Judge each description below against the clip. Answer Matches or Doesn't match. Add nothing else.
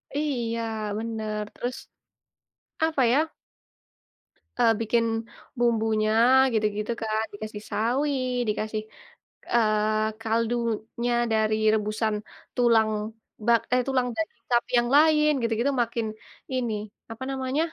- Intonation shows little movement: Matches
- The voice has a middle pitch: Doesn't match